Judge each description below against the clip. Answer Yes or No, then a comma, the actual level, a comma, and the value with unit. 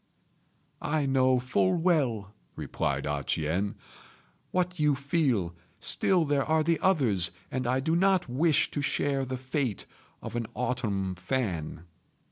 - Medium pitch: No, low, 130 Hz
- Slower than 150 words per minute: Yes, slow, 135 wpm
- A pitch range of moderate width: No, wide, 7.2 semitones